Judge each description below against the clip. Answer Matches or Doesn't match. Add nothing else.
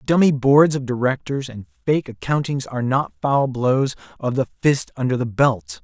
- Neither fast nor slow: Matches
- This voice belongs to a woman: Doesn't match